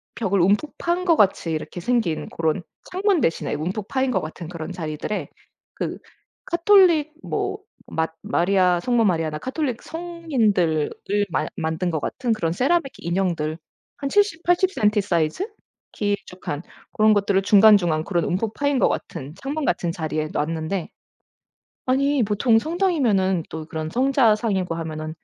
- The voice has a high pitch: Yes, high, 200 Hz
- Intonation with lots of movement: Yes, wide, 8.6 semitones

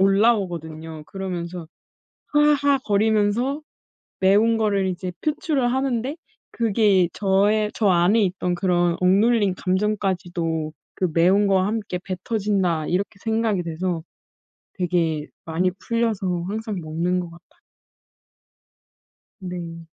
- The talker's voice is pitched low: No, high, 190 Hz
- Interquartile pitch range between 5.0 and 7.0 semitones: No, average, 3.7 semitones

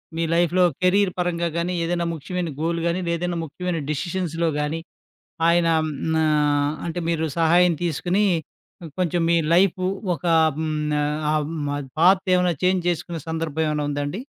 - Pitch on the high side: No, medium, 170 Hz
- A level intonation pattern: Yes, narrow, 1.9 semitones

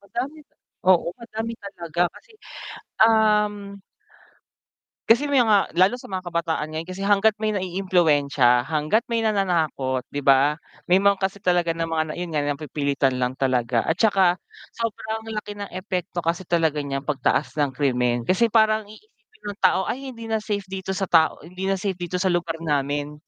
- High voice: No, medium, 180 Hz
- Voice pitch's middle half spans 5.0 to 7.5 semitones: Yes, wide, 5.6 semitones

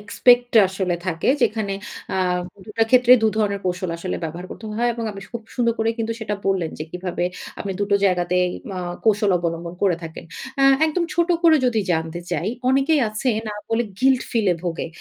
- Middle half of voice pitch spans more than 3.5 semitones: Yes, average, 4.8 semitones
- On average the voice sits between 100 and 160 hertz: No, high, 205 Hz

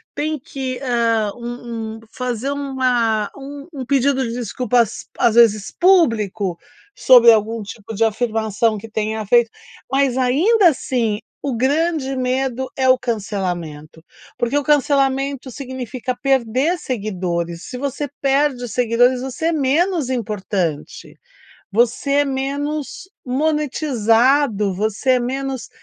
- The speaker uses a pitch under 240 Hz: No, very high, 250 Hz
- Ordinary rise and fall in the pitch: Yes, average, 3.7 semitones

